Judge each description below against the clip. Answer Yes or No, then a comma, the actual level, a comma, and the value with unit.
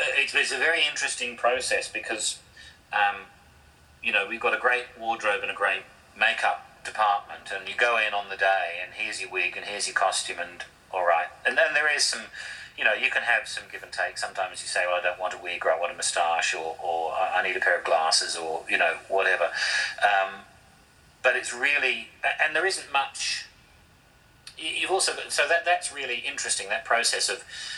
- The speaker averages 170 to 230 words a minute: Yes, fast, 205 wpm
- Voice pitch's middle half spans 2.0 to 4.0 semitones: No, average, 4.5 semitones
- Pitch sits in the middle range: No, very low, 95 Hz